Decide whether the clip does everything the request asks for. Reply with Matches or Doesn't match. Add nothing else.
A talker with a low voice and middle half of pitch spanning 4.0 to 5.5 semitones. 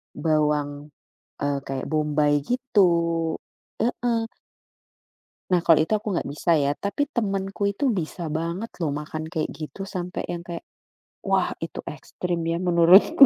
Doesn't match